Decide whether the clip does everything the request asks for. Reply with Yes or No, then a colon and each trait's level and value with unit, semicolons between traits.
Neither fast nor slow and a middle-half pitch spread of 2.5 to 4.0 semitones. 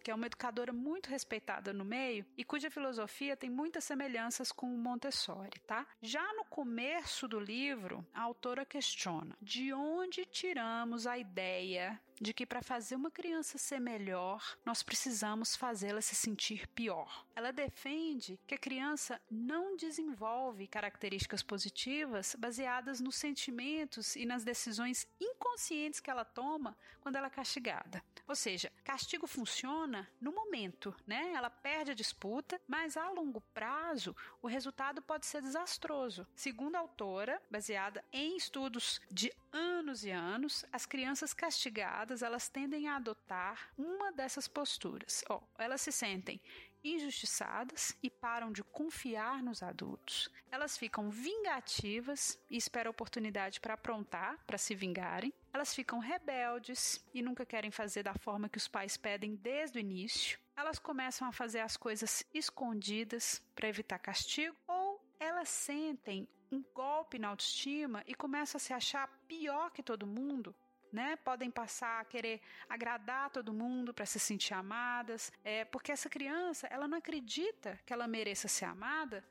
No: average, 150 wpm; average, 4.8 semitones